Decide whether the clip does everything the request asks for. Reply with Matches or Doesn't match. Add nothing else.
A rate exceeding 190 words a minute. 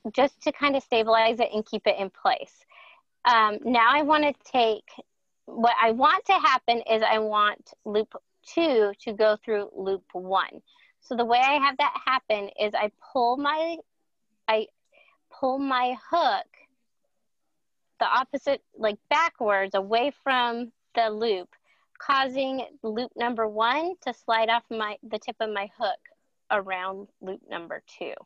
Doesn't match